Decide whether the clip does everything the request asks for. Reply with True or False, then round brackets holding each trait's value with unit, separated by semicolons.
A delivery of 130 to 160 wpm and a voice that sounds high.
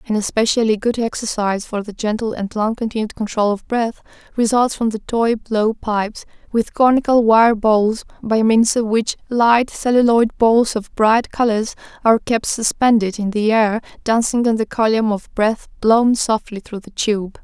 False (170 wpm; 220 Hz)